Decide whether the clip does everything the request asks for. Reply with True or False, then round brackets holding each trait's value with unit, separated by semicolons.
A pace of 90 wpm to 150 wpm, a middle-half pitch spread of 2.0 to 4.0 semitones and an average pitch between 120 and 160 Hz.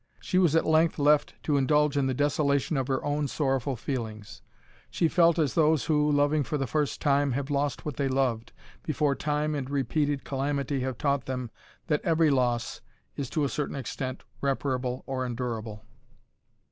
False (175 wpm; 2.4 semitones; 140 Hz)